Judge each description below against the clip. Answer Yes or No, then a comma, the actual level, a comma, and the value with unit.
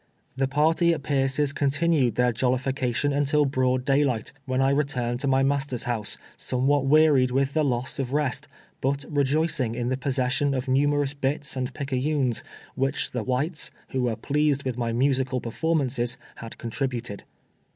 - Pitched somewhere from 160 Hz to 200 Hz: No, low, 135 Hz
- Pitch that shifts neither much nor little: No, narrow, 2.2 semitones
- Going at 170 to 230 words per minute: No, average, 160 wpm